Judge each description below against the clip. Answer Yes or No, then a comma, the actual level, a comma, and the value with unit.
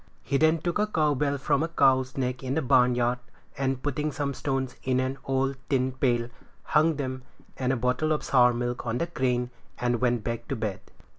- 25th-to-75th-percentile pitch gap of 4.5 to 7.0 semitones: No, average, 2.7 semitones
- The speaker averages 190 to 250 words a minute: Yes, fast, 205 wpm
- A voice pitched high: No, low, 130 Hz